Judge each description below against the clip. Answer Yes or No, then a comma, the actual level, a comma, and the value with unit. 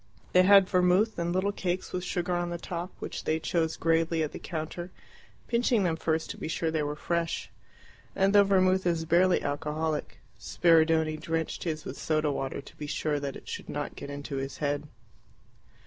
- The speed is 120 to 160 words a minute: No, average, 190 wpm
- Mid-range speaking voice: Yes, medium, 165 Hz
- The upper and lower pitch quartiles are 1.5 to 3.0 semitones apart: Yes, average, 2.7 semitones